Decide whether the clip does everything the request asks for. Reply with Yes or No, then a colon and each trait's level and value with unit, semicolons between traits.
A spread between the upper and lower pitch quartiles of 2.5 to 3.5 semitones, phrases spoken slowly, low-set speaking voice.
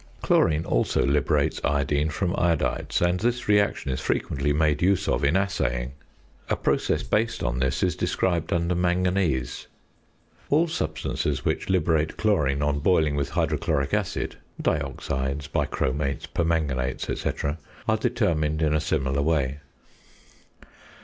No: average, 3.9 semitones; slow, 130 wpm; very low, 75 Hz